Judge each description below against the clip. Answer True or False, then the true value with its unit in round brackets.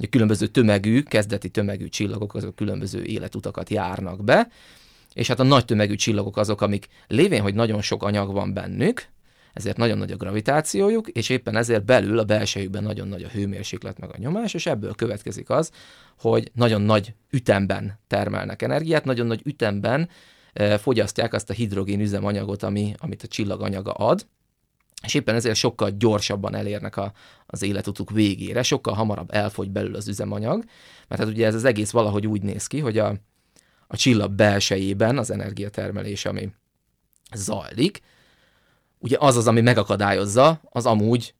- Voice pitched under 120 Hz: True (105 Hz)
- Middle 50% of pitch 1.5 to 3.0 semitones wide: True (2.5 semitones)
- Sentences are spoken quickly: True (160 wpm)